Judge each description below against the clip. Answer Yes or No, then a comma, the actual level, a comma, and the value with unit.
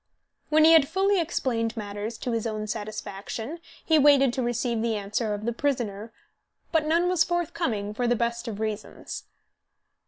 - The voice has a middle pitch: No, high, 235 Hz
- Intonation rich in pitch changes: Yes, wide, 5.8 semitones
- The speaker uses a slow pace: No, average, 165 wpm